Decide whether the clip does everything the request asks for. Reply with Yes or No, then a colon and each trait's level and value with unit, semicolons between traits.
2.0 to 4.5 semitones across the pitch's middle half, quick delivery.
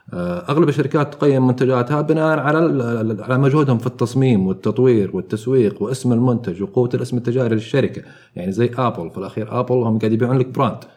Yes: average, 3.4 semitones; fast, 160 wpm